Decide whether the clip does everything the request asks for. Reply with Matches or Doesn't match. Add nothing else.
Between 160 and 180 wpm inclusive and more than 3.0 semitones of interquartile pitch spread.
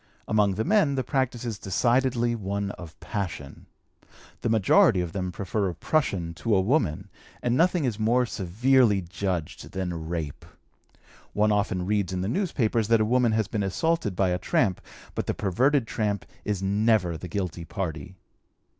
Matches